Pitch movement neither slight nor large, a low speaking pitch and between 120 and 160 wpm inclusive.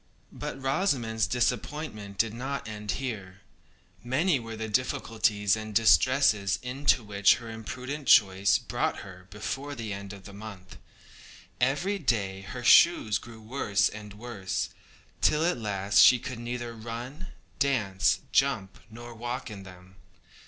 Yes: average, 4.2 semitones; low, 115 Hz; average, 140 wpm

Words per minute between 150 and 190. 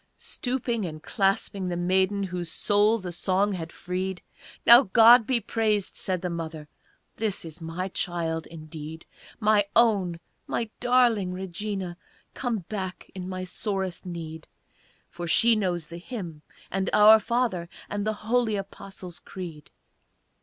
No: average, 140 wpm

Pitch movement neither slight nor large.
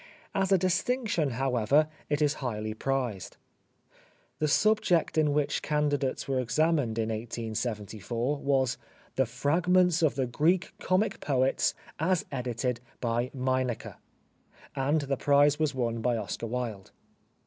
Yes: average, 4.4 semitones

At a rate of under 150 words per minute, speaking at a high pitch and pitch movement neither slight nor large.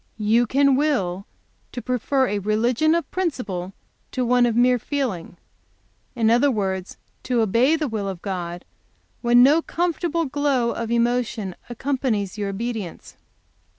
Yes: average, 140 wpm; high, 240 Hz; average, 4.9 semitones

